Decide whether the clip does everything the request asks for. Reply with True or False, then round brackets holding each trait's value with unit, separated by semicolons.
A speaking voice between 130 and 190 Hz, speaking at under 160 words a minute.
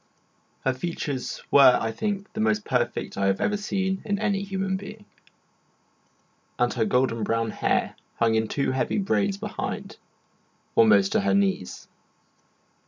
True (135 Hz; 145 wpm)